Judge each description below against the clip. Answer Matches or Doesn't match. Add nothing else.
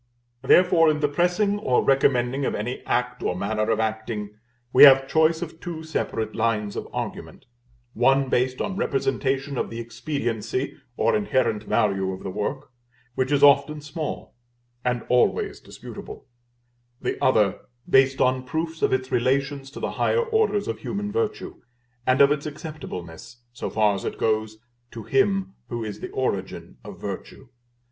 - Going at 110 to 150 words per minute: Doesn't match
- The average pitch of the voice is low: Matches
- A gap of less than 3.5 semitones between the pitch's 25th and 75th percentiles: Doesn't match